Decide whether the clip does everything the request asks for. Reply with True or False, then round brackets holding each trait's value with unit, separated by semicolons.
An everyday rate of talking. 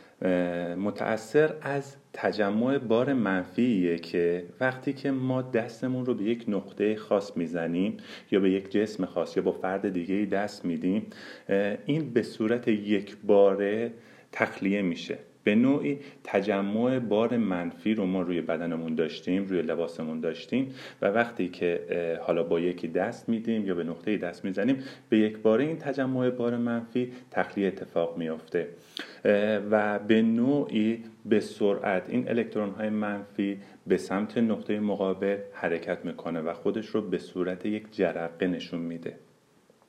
True (140 wpm)